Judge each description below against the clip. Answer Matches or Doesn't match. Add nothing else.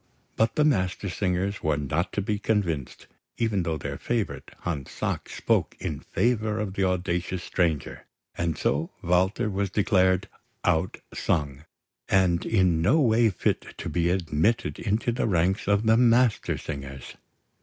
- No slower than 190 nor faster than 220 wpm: Doesn't match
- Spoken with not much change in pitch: Doesn't match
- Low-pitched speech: Matches